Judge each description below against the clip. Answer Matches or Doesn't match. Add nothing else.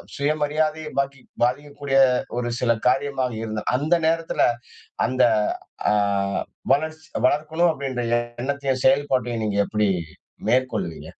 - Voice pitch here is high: Doesn't match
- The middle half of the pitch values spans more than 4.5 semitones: Doesn't match